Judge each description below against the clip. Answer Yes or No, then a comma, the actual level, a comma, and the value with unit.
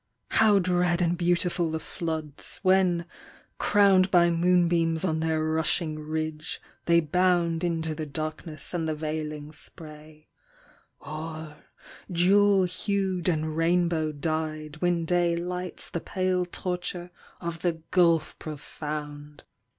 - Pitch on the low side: No, medium, 165 Hz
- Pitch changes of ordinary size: No, narrow, 2.2 semitones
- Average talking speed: No, slow, 120 wpm